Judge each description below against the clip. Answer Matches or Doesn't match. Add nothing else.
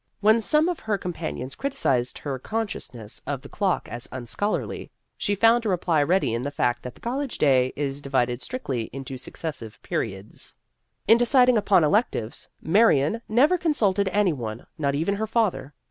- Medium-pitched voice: Matches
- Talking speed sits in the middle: Matches